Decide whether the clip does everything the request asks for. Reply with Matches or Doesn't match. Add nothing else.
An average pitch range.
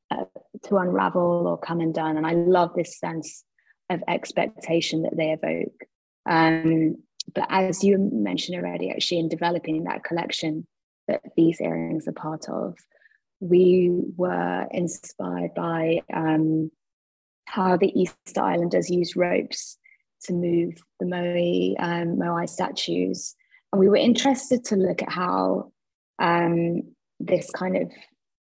Doesn't match